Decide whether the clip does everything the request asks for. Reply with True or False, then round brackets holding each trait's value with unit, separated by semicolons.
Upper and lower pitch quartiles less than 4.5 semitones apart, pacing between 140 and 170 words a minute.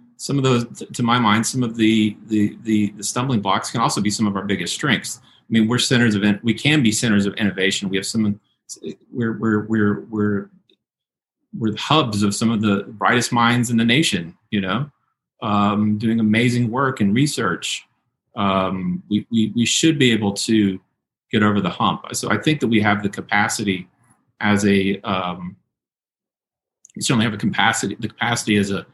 False (2.6 semitones; 195 wpm)